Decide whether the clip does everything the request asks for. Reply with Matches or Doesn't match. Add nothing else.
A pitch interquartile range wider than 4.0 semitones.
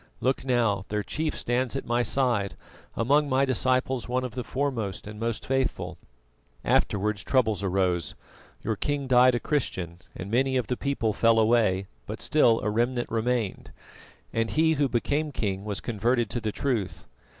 Doesn't match